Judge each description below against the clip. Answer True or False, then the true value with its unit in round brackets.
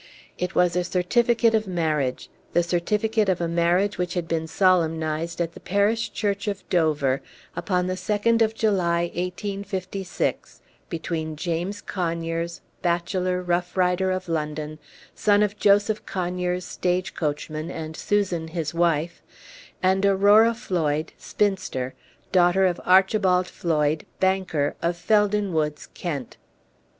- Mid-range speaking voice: True (180 Hz)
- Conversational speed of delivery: False (130 wpm)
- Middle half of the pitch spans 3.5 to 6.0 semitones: False (2.9 semitones)